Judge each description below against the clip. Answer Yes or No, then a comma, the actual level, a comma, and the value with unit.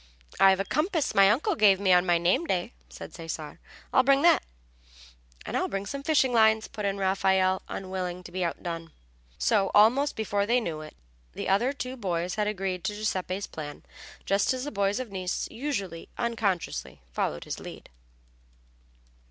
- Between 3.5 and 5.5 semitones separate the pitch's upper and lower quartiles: Yes, average, 4.1 semitones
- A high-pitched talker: Yes, high, 195 Hz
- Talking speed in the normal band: Yes, average, 170 wpm